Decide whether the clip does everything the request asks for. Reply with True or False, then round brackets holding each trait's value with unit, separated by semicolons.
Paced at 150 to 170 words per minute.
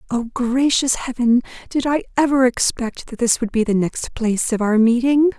False (190 wpm)